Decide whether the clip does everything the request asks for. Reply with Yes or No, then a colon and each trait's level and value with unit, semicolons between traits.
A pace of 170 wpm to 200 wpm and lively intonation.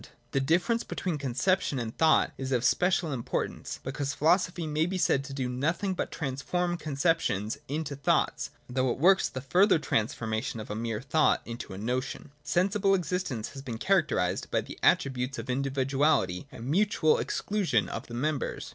Yes: average, 175 wpm; wide, 5.7 semitones